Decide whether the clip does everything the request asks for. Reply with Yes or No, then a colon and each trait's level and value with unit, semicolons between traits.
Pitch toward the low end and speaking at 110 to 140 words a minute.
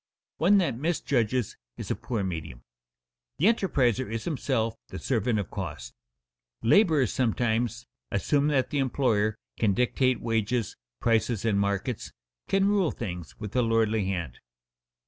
Yes: low, 115 Hz; slow, 135 wpm